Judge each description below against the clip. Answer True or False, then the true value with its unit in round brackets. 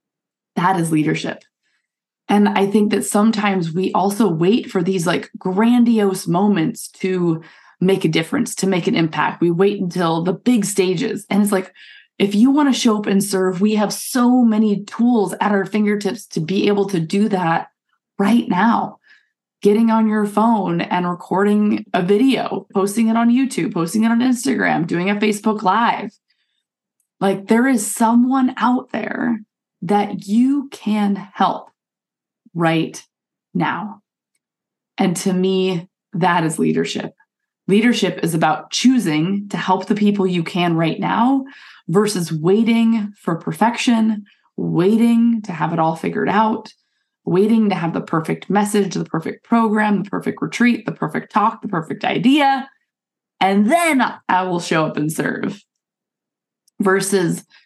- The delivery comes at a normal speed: True (150 wpm)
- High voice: True (205 Hz)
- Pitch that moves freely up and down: False (3.6 semitones)